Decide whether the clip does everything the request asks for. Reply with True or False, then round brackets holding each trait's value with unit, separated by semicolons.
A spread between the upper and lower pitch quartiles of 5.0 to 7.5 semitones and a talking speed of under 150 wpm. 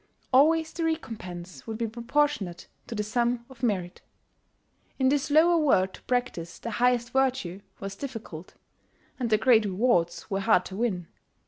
False (5.3 semitones; 155 wpm)